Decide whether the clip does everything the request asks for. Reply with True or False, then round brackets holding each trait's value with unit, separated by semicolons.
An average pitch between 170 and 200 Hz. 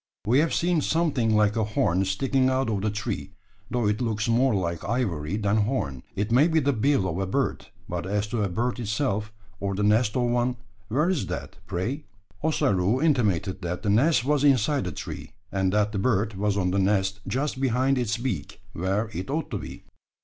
False (110 Hz)